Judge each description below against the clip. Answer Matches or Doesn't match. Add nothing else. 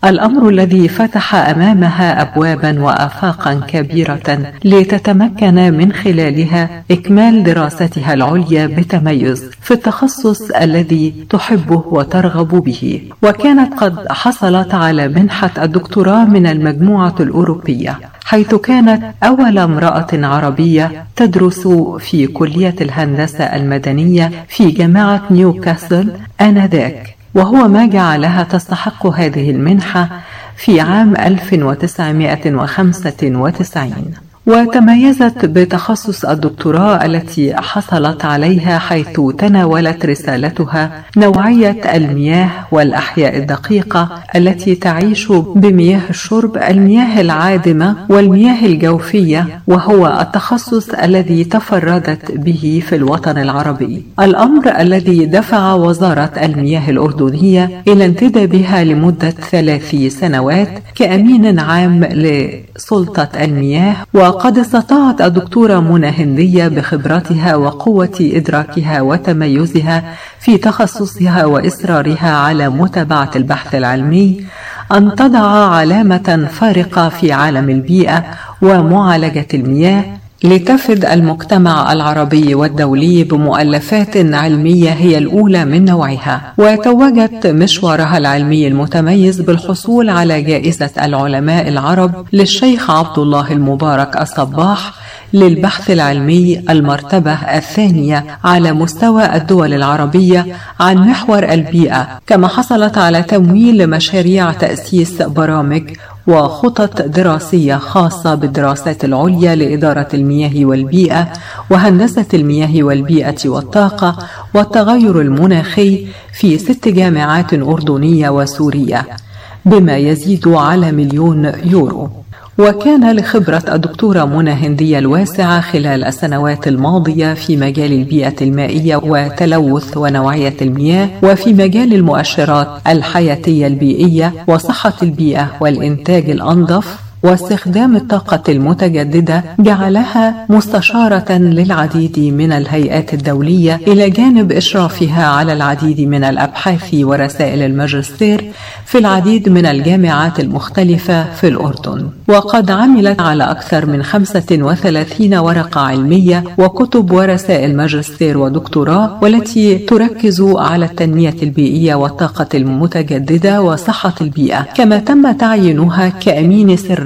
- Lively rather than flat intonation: Doesn't match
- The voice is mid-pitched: Matches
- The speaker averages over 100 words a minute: Doesn't match